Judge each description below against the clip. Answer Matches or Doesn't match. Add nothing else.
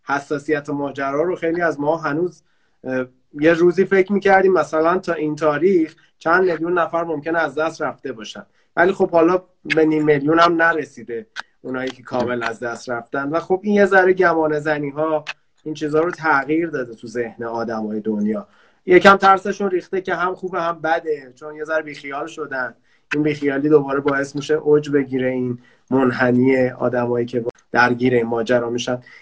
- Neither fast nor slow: Doesn't match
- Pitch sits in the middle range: Matches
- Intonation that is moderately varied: Matches